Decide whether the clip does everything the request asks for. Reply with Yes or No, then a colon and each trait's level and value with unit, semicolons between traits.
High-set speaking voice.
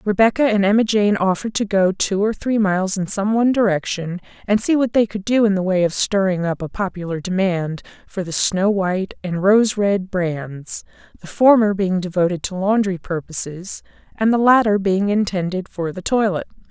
Yes: high, 195 Hz